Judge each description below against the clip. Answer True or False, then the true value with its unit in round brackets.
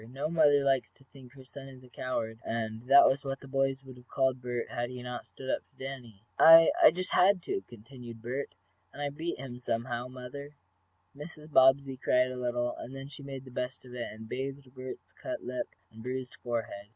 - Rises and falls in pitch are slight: True (2.1 semitones)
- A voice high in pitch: False (130 Hz)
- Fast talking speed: True (210 wpm)